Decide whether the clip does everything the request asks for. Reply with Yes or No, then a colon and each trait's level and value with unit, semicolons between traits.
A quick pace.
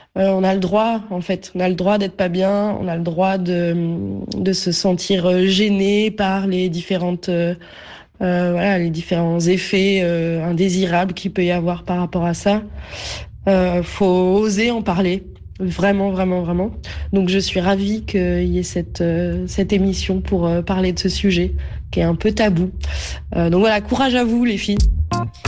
No: average, 185 wpm